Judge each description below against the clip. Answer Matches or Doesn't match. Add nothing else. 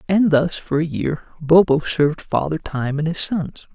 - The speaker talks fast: Doesn't match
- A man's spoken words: Matches